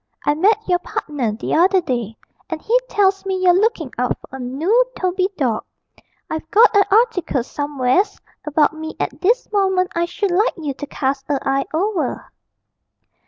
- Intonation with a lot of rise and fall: Yes, wide, 5.7 semitones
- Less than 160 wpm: No, average, 170 wpm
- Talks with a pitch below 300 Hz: No, very high, 340 Hz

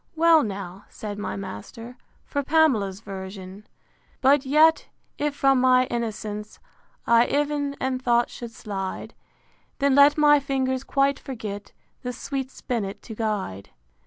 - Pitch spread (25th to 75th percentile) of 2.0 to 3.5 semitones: No, average, 5.2 semitones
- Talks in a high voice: Yes, high, 245 Hz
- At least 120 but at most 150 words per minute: Yes, slow, 135 wpm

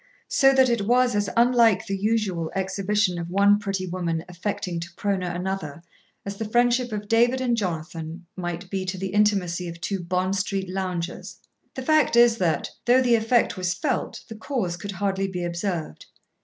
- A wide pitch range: No, average, 4.0 semitones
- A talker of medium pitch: No, high, 195 Hz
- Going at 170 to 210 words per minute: Yes, average, 180 wpm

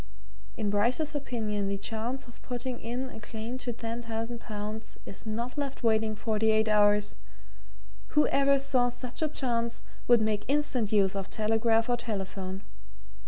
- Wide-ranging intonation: No, narrow, 2.6 semitones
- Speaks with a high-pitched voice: Yes, high, 225 Hz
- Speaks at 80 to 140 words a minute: No, average, 155 wpm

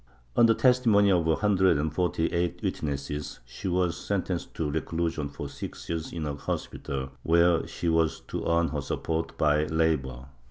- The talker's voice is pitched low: Yes, very low, 80 Hz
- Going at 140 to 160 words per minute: No, average, 170 wpm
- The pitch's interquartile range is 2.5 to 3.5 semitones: Yes, average, 3.0 semitones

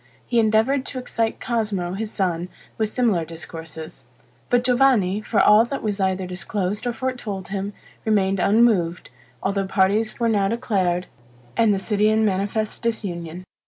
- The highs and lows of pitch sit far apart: No, average, 3.2 semitones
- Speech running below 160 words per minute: Yes, average, 150 wpm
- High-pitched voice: Yes, high, 205 Hz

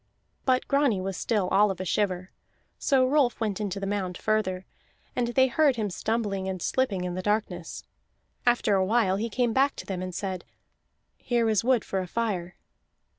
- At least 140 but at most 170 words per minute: No, average, 185 wpm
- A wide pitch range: No, average, 4.3 semitones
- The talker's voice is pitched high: Yes, high, 205 Hz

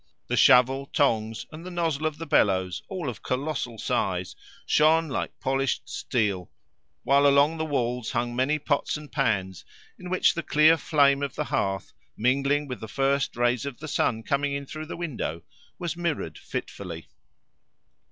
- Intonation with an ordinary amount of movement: Yes, average, 4.3 semitones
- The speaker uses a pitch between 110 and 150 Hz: Yes, medium, 140 Hz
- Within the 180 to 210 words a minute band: No, average, 165 wpm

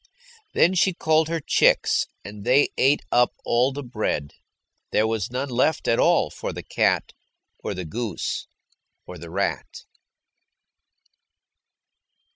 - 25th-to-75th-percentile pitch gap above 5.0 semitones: Yes, wide, 5.4 semitones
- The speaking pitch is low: Yes, low, 125 Hz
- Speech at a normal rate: No, slow, 130 wpm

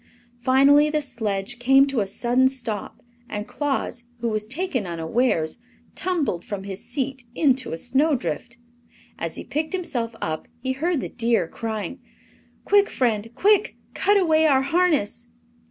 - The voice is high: Yes, very high, 255 Hz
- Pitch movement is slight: No, wide, 5.5 semitones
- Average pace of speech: Yes, average, 145 wpm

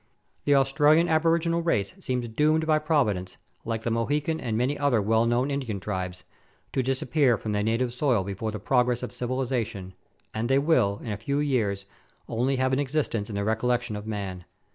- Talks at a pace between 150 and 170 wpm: No, average, 185 wpm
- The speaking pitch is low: Yes, low, 125 Hz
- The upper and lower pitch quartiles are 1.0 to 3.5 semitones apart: No, average, 5.0 semitones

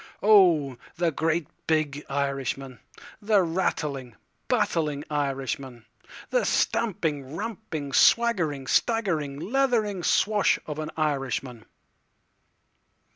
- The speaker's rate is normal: No, slow, 80 wpm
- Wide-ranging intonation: Yes, wide, 5.8 semitones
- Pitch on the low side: No, medium, 155 Hz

